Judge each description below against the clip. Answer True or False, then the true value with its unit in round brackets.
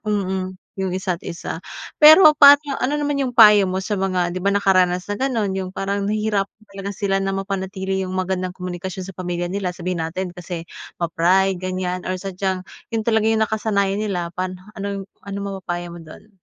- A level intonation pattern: True (1.9 semitones)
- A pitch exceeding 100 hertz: True (190 Hz)